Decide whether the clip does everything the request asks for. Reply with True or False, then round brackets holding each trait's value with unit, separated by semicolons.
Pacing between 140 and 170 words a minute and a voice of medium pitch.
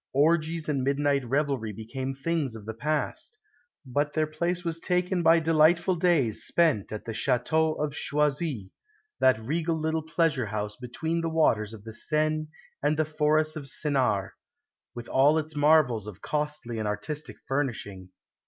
True (155 wpm; 150 Hz)